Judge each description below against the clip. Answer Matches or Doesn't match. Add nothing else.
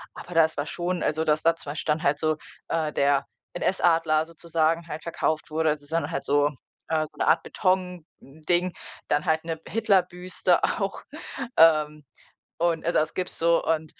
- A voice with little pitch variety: Matches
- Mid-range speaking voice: Matches